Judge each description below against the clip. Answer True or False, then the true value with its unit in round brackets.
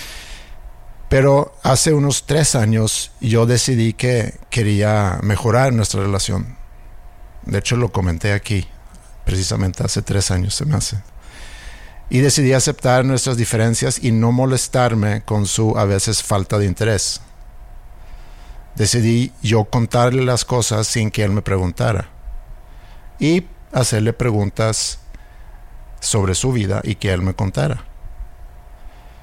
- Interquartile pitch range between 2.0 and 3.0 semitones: False (3.8 semitones)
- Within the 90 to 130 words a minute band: True (125 wpm)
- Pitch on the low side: True (110 Hz)